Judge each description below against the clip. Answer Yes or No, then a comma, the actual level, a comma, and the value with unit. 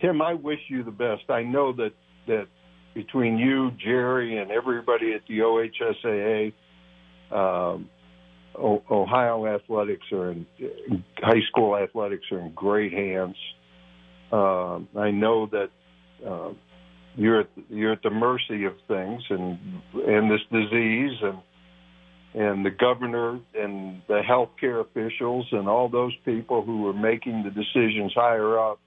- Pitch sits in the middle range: No, low, 105 Hz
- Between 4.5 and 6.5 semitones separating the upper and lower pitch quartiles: Yes, average, 4.8 semitones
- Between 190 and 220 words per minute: No, average, 140 wpm